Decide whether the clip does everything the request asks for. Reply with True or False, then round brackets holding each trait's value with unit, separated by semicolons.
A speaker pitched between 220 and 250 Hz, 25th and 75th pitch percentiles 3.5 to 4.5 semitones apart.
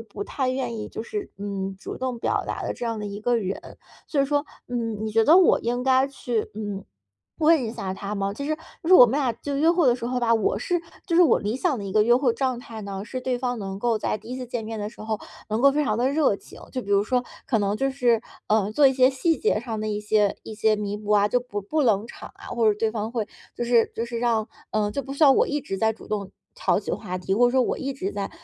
True (230 Hz; 3.8 semitones)